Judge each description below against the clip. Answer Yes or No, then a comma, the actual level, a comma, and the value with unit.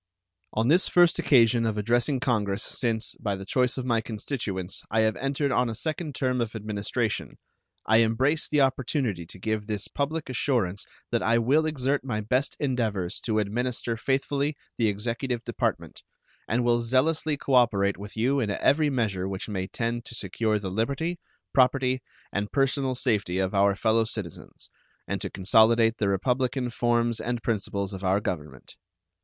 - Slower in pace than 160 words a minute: No, average, 165 wpm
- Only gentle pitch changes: No, average, 4.1 semitones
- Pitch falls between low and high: No, low, 115 Hz